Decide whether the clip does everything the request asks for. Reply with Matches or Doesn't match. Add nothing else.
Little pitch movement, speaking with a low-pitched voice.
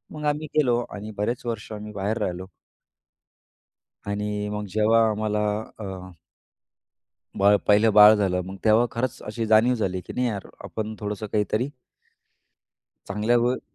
Matches